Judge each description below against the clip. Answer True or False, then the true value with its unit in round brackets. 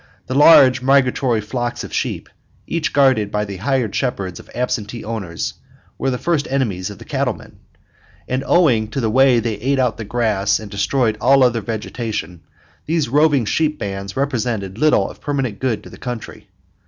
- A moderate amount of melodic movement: True (4.3 semitones)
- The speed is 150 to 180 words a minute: True (175 wpm)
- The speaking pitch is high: False (120 Hz)